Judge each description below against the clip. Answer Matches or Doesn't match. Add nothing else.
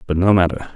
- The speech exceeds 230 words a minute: Matches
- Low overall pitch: Matches